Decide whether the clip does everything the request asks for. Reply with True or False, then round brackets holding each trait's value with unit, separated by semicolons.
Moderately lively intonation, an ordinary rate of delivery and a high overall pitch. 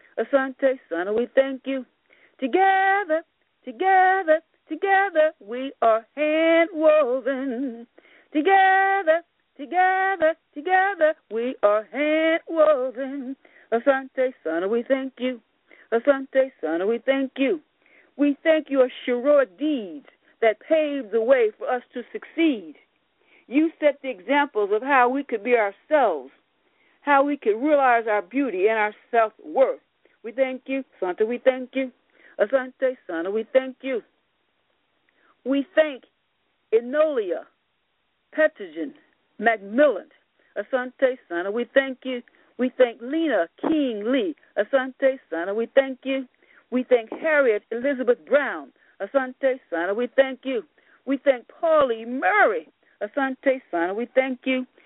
False (4.0 semitones; 125 wpm; 270 Hz)